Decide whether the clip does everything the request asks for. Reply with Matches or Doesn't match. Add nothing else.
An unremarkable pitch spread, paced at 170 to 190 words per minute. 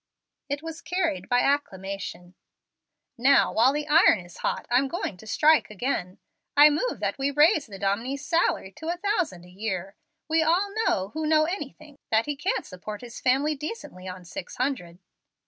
Doesn't match